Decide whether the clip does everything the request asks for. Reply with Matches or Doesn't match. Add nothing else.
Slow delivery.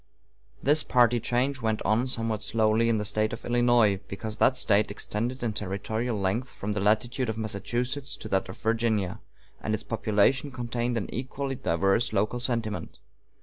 Doesn't match